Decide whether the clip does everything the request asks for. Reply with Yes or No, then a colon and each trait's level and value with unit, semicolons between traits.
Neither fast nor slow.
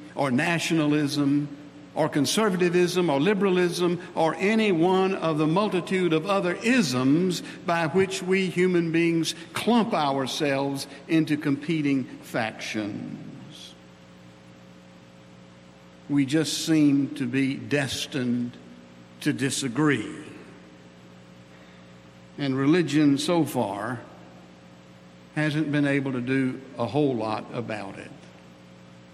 No: slow, 95 wpm